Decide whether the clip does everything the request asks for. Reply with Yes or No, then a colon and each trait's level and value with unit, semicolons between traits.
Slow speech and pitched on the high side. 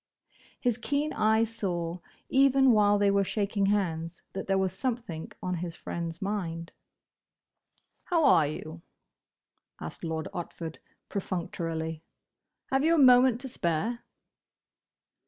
Yes: slow, 120 wpm; high, 195 Hz